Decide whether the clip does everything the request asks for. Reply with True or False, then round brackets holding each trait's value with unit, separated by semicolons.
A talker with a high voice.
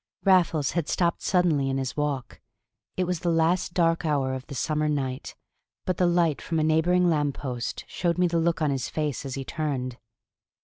False (155 Hz)